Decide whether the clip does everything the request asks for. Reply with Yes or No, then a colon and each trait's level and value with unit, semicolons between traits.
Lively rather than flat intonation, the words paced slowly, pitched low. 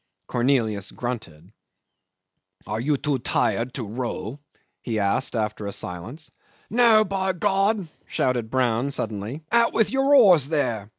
Yes: wide, 8.7 semitones; slow, 130 wpm; low, 130 Hz